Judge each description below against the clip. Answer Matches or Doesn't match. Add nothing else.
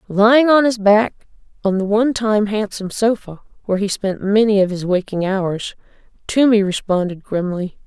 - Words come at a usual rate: Matches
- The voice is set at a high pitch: Matches